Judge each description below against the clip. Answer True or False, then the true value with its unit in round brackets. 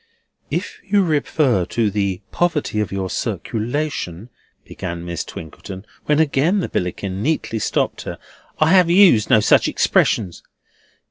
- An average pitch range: False (8.6 semitones)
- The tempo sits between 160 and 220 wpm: False (135 wpm)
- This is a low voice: True (115 Hz)